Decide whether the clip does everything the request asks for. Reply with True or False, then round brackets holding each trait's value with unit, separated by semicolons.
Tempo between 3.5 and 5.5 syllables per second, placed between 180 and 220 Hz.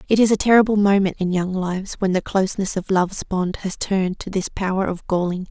False (5.9 syllables/s; 190 Hz)